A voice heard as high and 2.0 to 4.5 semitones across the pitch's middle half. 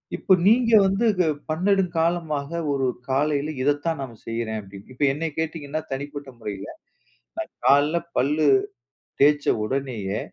No: medium, 145 Hz; average, 3.6 semitones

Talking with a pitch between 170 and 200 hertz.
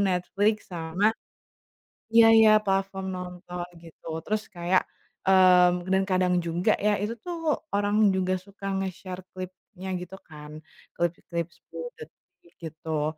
Yes: medium, 185 Hz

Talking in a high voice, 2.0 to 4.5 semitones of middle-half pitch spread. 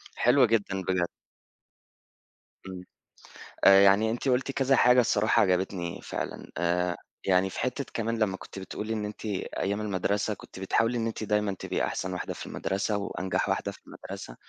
No: low, 100 Hz; average, 3.2 semitones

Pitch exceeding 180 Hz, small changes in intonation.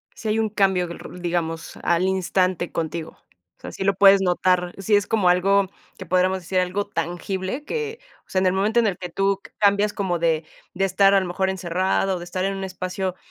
Yes: high, 190 Hz; narrow, 1.8 semitones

